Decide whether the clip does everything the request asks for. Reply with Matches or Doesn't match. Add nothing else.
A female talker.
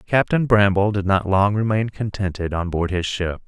Doesn't match